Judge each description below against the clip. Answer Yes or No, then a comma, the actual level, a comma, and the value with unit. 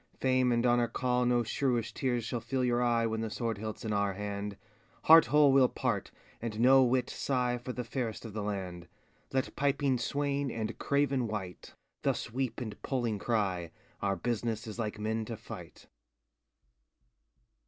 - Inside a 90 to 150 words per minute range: No, average, 170 wpm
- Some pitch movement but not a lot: Yes, average, 3.0 semitones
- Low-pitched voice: Yes, low, 120 Hz